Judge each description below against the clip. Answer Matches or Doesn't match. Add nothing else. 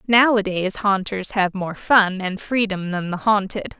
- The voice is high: Matches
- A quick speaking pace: Doesn't match